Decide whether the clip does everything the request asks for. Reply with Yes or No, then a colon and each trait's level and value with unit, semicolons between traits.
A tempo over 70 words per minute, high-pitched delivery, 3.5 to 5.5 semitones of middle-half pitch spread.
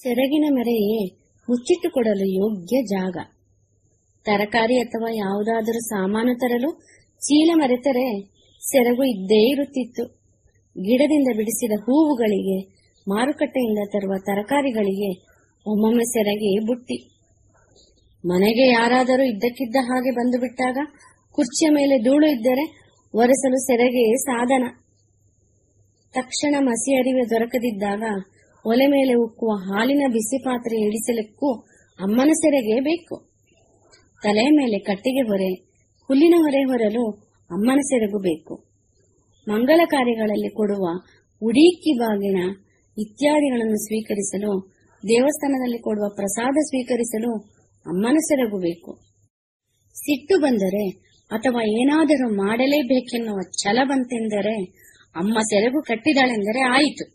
Yes: average, 90 wpm; high, 230 Hz; average, 4.6 semitones